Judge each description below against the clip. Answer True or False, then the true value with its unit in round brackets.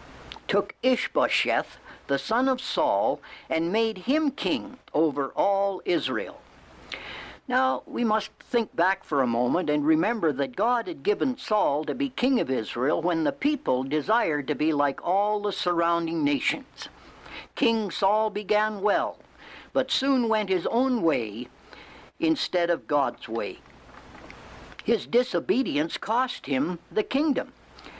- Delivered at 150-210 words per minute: False (135 wpm)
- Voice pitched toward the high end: True (220 Hz)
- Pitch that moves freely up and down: True (7.3 semitones)